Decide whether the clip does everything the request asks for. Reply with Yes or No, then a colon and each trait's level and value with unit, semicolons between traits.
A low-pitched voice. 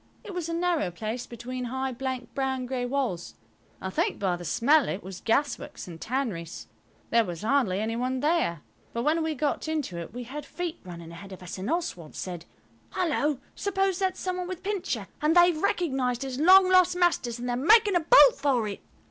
No: very high, 265 Hz